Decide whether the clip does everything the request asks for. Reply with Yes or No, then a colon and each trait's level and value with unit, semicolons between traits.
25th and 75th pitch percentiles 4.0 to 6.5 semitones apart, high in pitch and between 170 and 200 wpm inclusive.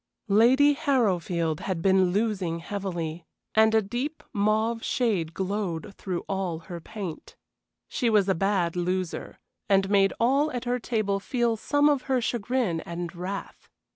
No: average, 4.8 semitones; high, 200 Hz; average, 145 wpm